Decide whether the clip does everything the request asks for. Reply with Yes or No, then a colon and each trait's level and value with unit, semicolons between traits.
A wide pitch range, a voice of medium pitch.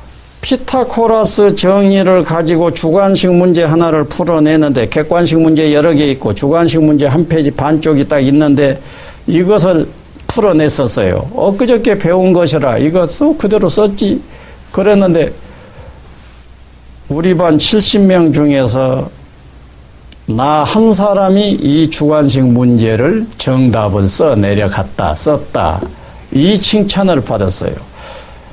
Yes: wide, 6.6 semitones; medium, 155 Hz